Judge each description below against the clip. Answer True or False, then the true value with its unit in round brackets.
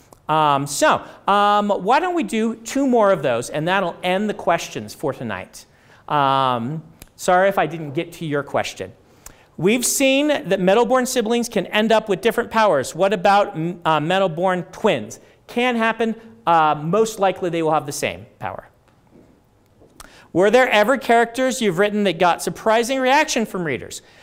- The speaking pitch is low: False (195 Hz)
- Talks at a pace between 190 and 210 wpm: False (165 wpm)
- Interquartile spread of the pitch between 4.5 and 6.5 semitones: True (5.3 semitones)